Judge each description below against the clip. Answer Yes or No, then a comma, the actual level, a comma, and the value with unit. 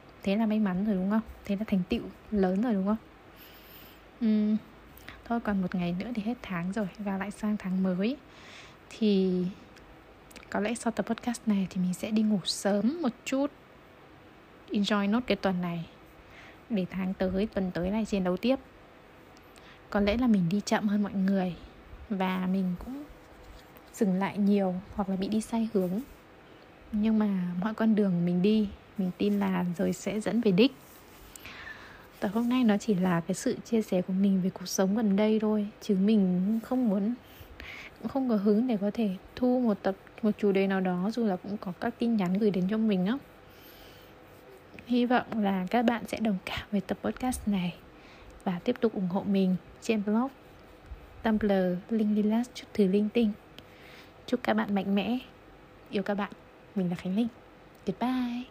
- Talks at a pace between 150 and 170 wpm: No, average, 190 wpm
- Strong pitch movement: No, average, 2.7 semitones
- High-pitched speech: Yes, high, 205 Hz